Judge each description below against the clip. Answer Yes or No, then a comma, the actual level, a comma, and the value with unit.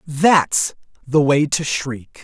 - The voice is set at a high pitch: No, medium, 145 Hz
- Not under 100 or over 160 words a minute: Yes, slow, 135 wpm